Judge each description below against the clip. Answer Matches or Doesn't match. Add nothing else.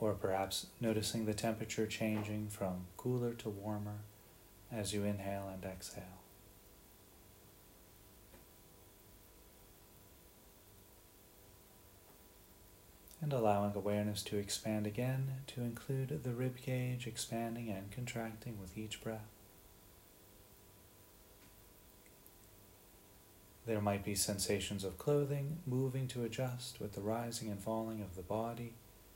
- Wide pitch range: Doesn't match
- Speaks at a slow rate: Matches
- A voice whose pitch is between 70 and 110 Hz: Matches